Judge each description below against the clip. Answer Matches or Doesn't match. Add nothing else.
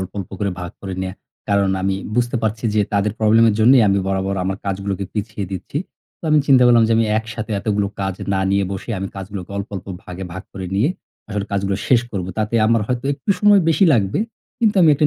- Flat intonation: Doesn't match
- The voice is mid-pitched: Doesn't match